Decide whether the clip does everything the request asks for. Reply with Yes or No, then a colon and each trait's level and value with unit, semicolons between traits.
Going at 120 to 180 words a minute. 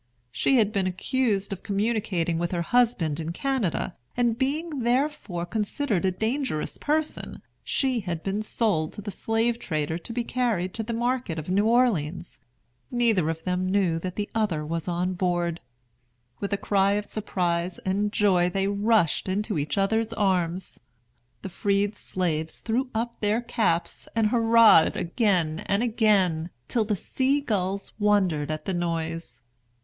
Yes: average, 155 wpm